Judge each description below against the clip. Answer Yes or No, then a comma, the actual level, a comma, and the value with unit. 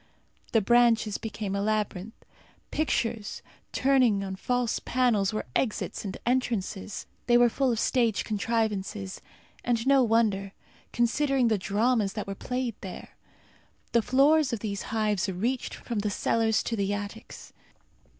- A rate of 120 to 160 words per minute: Yes, average, 140 wpm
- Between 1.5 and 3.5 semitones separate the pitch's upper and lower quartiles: Yes, average, 3.1 semitones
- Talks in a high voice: Yes, high, 225 Hz